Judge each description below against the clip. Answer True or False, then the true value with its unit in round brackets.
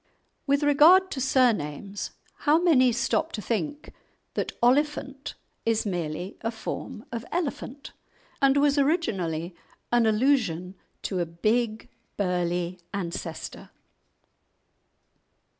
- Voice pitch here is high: True (230 Hz)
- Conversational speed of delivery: False (105 wpm)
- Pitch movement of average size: False (7.6 semitones)